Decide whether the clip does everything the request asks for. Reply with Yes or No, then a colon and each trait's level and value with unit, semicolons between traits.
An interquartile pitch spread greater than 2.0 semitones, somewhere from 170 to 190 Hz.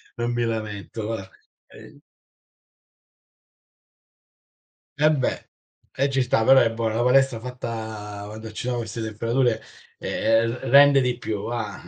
No: narrow, 2.4 semitones; low, 115 Hz